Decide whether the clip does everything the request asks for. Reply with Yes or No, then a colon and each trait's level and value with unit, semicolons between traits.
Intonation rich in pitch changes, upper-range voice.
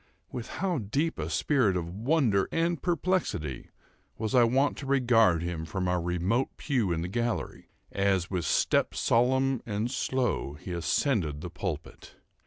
No: wide, 7.2 semitones; low, 110 Hz